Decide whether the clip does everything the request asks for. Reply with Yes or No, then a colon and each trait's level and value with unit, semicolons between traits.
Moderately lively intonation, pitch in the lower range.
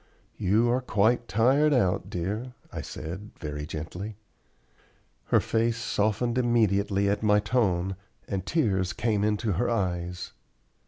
Yes: average, 4.0 semitones; low, 105 Hz